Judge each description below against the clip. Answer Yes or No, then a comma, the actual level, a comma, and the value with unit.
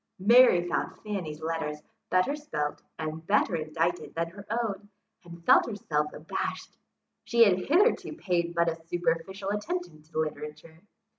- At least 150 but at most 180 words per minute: No, average, 140 wpm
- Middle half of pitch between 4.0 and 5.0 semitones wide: Yes, average, 4.4 semitones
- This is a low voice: No, medium, 175 Hz